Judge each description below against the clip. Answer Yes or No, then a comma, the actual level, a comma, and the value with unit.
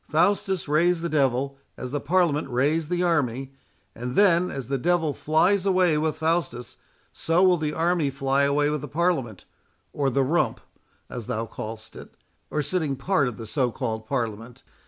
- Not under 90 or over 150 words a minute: No, average, 175 wpm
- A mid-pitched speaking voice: Yes, medium, 145 Hz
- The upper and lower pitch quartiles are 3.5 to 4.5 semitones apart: No, average, 5.0 semitones